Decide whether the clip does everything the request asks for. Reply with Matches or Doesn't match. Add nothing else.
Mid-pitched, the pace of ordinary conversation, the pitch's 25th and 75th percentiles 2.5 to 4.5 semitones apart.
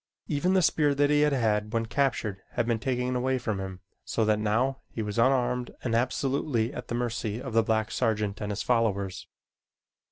Doesn't match